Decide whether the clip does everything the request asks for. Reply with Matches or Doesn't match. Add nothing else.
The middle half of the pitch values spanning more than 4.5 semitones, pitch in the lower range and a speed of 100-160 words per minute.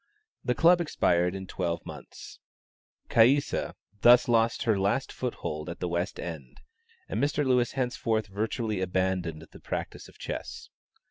Matches